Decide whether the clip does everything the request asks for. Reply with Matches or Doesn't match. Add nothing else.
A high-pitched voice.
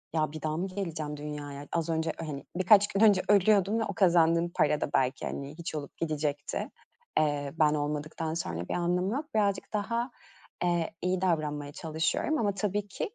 Doesn't match